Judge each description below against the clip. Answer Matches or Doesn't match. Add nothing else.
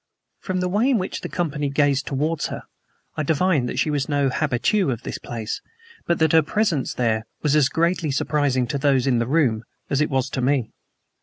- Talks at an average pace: Doesn't match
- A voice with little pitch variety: Doesn't match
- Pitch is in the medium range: Matches